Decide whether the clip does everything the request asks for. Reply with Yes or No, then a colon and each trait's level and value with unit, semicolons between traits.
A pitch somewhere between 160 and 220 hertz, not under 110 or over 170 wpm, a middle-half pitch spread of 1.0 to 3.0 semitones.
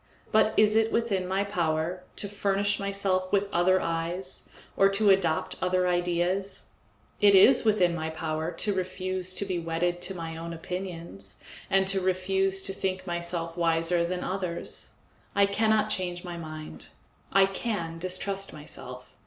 Yes: medium, 185 Hz; average, 155 wpm; narrow, 2.6 semitones